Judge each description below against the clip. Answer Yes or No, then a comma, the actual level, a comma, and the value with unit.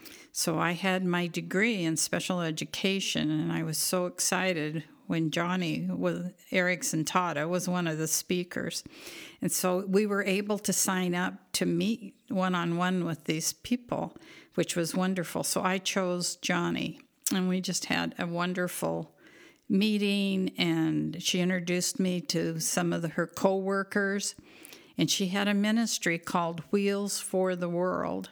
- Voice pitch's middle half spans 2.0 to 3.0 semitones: Yes, narrow, 2.5 semitones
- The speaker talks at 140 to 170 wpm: Yes, average, 150 wpm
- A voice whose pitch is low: No, medium, 180 Hz